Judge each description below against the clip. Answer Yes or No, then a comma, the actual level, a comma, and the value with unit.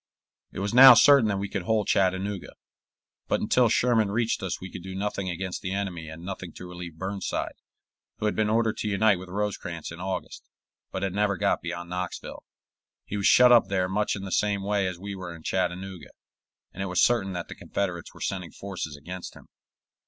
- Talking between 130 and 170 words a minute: No, fast, 205 wpm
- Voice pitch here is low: Yes, very low, 95 Hz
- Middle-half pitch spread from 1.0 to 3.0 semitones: Yes, narrow, 2.4 semitones